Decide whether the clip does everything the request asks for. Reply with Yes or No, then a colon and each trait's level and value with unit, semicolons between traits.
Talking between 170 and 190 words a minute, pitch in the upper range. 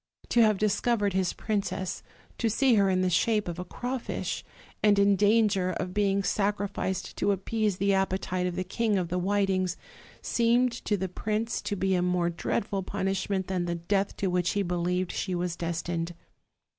Yes: average, 180 wpm; high, 195 Hz